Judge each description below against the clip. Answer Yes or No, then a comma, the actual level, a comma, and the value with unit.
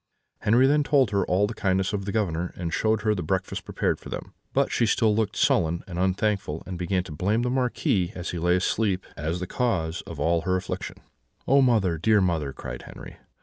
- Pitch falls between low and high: No, very low, 95 Hz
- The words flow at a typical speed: No, fast, 215 wpm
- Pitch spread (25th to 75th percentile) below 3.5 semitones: No, average, 3.8 semitones